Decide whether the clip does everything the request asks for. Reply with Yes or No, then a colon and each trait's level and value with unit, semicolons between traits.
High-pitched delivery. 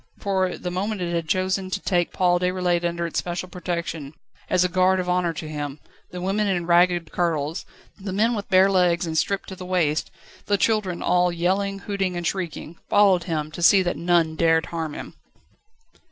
No: medium, 180 Hz